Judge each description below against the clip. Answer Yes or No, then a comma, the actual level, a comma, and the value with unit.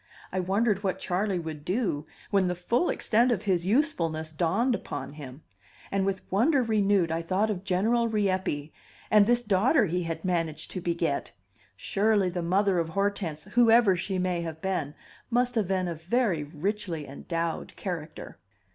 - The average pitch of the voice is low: No, medium, 185 Hz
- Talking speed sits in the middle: Yes, average, 165 wpm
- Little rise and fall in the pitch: No, average, 4.2 semitones